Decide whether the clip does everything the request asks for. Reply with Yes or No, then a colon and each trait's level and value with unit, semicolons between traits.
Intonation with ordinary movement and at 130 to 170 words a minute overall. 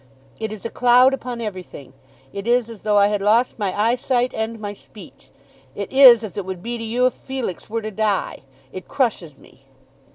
No: average, 3.3 semitones; average, 200 wpm